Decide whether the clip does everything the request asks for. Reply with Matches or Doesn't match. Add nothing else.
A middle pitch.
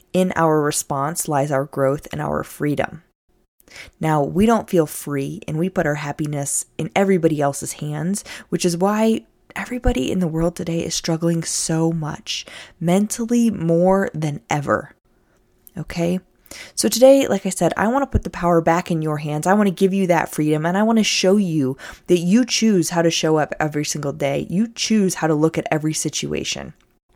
Matches